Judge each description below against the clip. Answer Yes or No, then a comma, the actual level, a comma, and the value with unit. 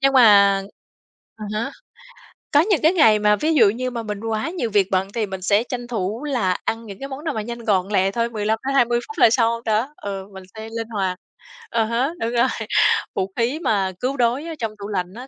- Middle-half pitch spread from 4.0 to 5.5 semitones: No, average, 3.6 semitones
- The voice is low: No, high, 225 Hz